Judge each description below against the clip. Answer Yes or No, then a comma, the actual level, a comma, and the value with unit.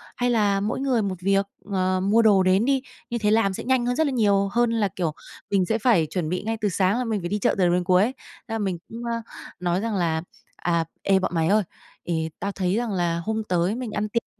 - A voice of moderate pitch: No, high, 200 Hz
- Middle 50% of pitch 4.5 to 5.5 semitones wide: No, average, 3.8 semitones